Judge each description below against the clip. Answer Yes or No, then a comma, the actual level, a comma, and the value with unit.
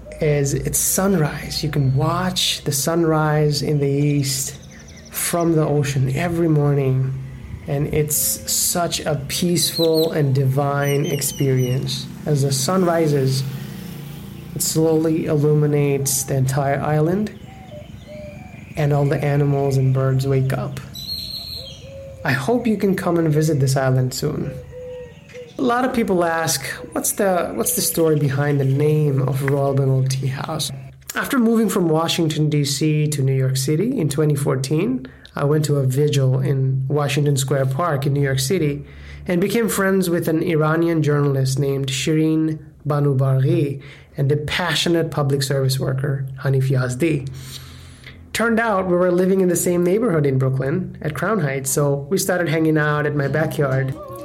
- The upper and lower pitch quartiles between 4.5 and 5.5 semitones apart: No, average, 3.2 semitones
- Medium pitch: Yes, medium, 150 Hz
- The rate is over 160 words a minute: No, average, 150 wpm